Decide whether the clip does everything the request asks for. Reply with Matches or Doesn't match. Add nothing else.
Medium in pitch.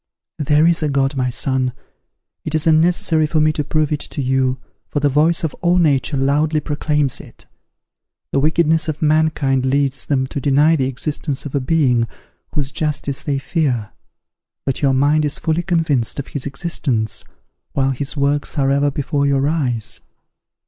Matches